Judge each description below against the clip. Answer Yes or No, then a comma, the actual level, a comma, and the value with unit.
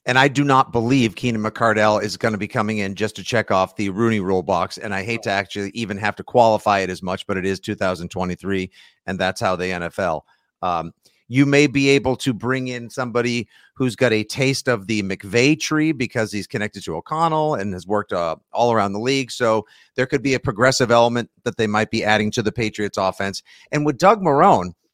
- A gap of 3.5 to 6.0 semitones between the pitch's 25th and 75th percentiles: Yes, average, 4.2 semitones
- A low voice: Yes, low, 110 Hz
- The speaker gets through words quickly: Yes, fast, 220 wpm